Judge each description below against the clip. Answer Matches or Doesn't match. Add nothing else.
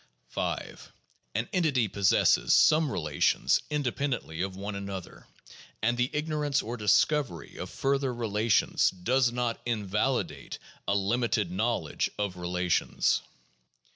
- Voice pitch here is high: Doesn't match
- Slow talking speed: Matches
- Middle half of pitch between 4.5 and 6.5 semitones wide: Matches